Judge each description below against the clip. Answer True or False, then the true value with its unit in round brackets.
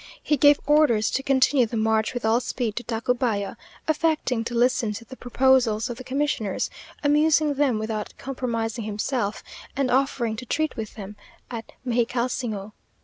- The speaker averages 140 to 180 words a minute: True (155 wpm)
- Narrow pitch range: False (3.3 semitones)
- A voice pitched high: True (245 Hz)